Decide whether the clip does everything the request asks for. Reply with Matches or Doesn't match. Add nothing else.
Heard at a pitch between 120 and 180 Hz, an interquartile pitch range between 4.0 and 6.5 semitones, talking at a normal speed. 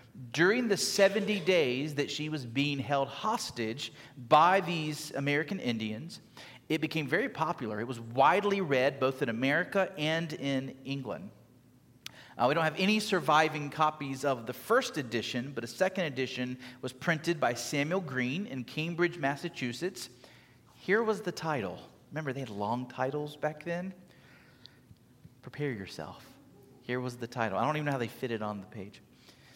Matches